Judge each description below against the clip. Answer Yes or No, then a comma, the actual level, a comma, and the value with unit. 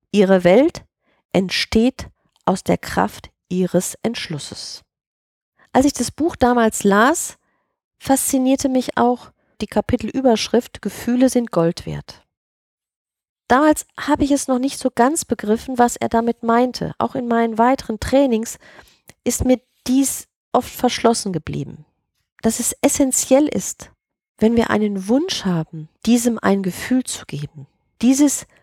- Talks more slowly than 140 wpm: Yes, average, 130 wpm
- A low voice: No, high, 240 Hz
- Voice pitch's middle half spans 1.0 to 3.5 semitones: No, average, 4.0 semitones